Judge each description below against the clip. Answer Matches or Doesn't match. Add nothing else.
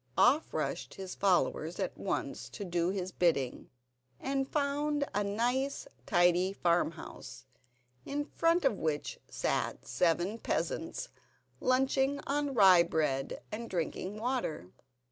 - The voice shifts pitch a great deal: Matches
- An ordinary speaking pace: Doesn't match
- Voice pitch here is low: Doesn't match